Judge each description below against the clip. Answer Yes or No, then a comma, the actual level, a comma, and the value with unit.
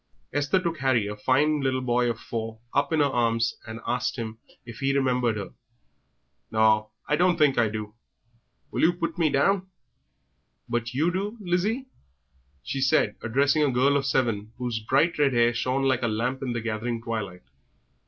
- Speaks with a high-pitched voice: No, low, 130 Hz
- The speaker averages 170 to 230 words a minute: Yes, average, 180 wpm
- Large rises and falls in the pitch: No, average, 4.2 semitones